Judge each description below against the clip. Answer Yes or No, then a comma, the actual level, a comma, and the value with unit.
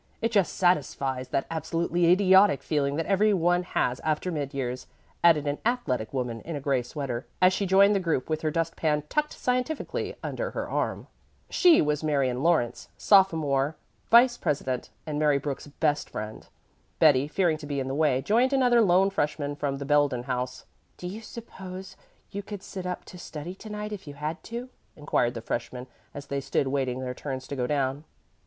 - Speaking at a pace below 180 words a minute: No, average, 190 wpm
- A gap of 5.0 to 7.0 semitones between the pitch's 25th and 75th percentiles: Yes, wide, 5.6 semitones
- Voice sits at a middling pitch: Yes, medium, 155 Hz